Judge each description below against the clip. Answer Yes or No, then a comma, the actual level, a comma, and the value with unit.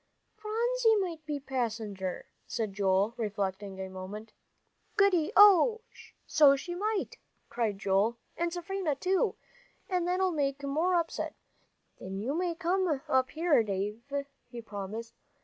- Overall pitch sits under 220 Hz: No, very high, 275 Hz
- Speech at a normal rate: No, slow, 130 wpm